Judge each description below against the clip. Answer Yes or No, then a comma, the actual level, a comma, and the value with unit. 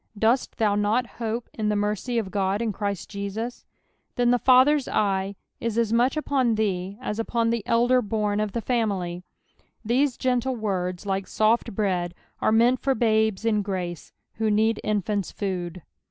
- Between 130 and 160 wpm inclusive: No, average, 170 wpm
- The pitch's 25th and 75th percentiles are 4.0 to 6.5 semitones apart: No, average, 2.8 semitones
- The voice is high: Yes, high, 215 Hz